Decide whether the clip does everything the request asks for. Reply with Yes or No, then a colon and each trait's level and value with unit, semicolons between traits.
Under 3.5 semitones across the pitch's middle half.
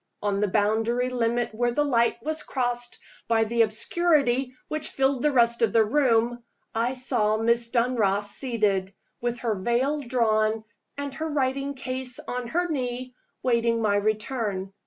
Yes: average, 2.8 semitones